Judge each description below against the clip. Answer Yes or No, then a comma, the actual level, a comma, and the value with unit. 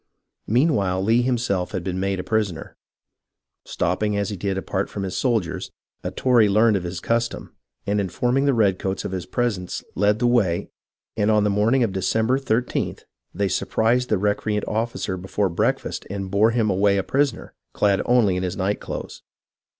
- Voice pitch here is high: No, low, 105 Hz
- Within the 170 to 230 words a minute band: Yes, average, 180 wpm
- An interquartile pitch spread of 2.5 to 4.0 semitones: Yes, average, 3.4 semitones